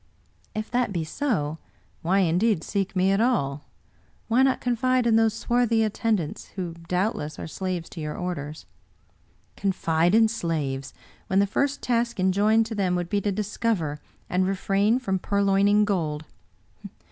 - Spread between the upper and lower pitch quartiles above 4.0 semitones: Yes, average, 4.7 semitones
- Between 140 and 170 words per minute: Yes, average, 160 wpm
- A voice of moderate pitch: No, high, 195 Hz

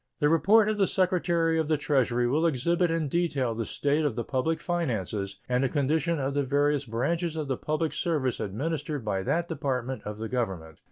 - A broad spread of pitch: No, average, 4.8 semitones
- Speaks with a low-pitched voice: No, medium, 145 Hz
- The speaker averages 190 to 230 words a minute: Yes, average, 200 wpm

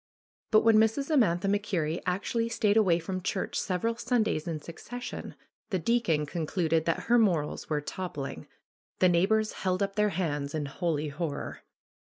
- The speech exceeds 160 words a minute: No, average, 155 wpm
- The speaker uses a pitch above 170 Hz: Yes, medium, 185 Hz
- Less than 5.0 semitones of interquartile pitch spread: No, average, 5.3 semitones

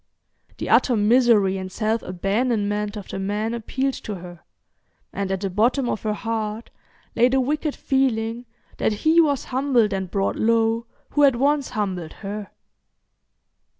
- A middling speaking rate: Yes, average, 150 wpm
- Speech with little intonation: No, average, 3.7 semitones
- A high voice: Yes, high, 225 Hz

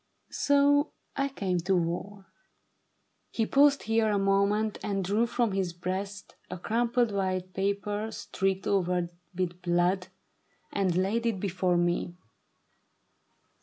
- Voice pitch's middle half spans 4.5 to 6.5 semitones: No, average, 3.2 semitones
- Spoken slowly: Yes, slow, 130 wpm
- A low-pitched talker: No, high, 195 Hz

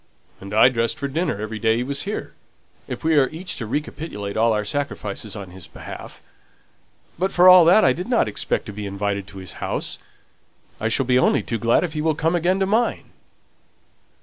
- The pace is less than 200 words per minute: No, fast, 205 wpm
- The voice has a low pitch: Yes, low, 125 Hz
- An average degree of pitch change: No, wide, 7.8 semitones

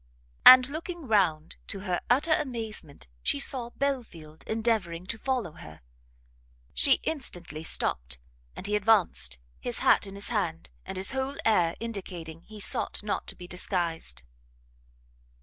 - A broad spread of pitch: Yes, wide, 6.2 semitones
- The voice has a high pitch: Yes, high, 195 Hz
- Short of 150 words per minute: Yes, average, 140 wpm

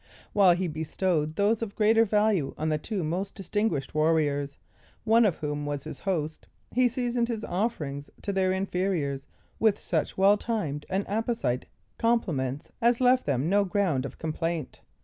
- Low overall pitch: No, medium, 185 Hz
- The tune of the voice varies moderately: No, wide, 6.1 semitones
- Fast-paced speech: No, average, 160 wpm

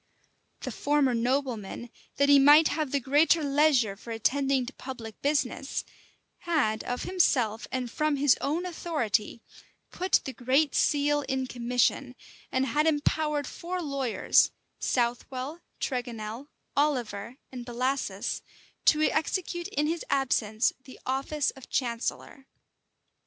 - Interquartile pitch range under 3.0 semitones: No, average, 3.5 semitones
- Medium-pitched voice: No, very high, 270 Hz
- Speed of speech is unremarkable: No, slow, 125 wpm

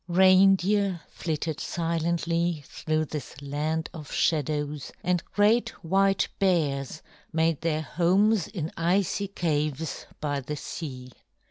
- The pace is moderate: No, slow, 110 wpm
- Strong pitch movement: No, average, 3.6 semitones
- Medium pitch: Yes, medium, 165 Hz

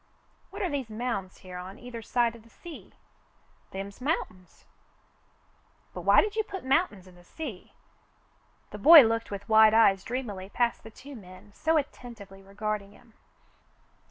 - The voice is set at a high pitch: Yes, high, 225 Hz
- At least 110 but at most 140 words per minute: No, average, 155 wpm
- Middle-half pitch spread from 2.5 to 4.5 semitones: No, average, 4.9 semitones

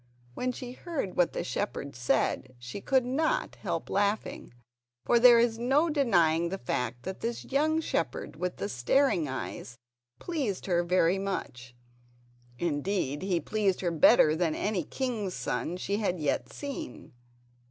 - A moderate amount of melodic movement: No, wide, 7.4 semitones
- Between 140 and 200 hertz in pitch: Yes, high, 190 Hz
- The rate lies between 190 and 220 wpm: No, average, 150 wpm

